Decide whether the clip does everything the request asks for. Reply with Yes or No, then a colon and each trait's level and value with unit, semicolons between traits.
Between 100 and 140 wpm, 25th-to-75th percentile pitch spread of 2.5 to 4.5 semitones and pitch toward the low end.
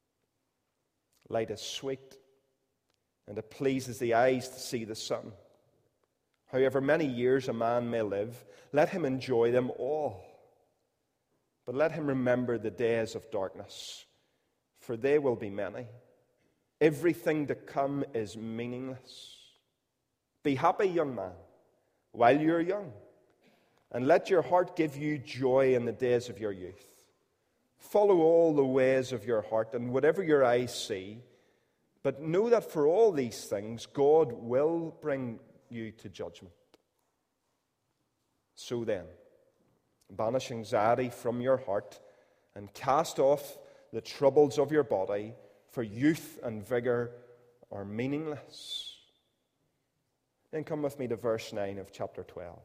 Yes: slow, 135 wpm; average, 3.7 semitones; low, 125 Hz